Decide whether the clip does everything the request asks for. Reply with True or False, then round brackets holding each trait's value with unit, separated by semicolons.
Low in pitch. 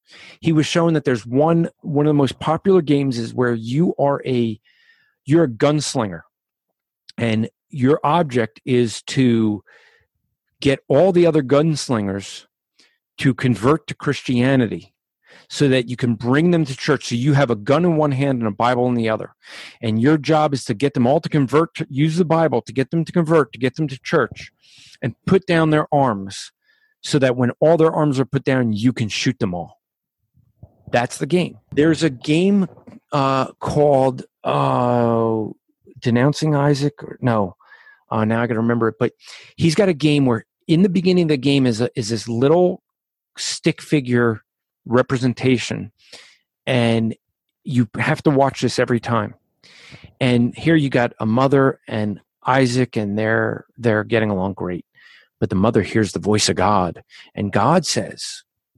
True (130 Hz)